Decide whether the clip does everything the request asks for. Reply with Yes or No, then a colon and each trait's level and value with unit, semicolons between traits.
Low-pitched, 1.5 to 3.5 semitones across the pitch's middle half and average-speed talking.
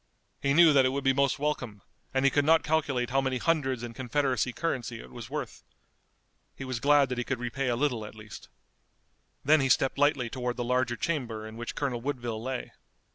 No: low, 130 Hz; average, 2.7 semitones; fast, 210 wpm